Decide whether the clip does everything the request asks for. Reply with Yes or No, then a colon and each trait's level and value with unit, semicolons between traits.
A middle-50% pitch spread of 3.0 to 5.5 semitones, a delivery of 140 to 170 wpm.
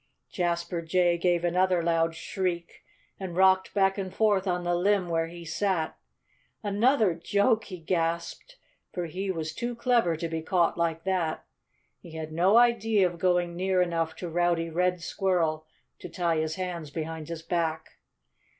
No: narrow, 2.4 semitones; average, 160 wpm